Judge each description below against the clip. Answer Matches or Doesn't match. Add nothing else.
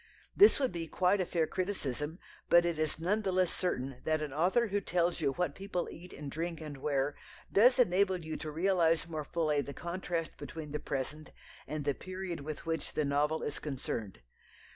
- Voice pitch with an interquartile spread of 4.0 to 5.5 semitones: Doesn't match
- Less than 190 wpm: Doesn't match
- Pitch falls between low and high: Matches